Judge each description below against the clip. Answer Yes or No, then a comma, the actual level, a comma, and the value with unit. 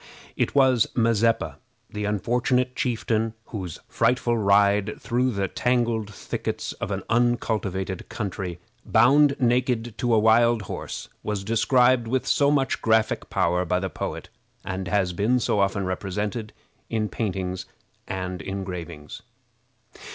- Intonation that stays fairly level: No, average, 3.8 semitones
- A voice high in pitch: No, low, 110 Hz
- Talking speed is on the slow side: Yes, slow, 130 wpm